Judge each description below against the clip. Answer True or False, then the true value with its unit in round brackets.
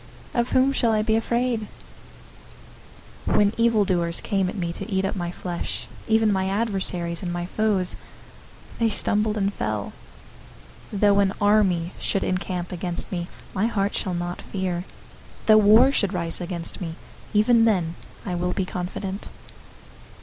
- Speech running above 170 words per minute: False (155 wpm)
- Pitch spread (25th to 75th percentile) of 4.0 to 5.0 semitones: False (3.4 semitones)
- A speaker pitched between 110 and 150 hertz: False (195 Hz)